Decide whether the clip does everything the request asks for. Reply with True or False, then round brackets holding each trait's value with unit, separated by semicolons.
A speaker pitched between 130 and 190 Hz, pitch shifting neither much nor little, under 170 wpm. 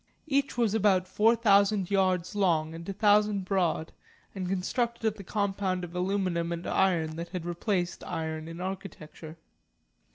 True (185 Hz; 3.1 semitones; 155 wpm)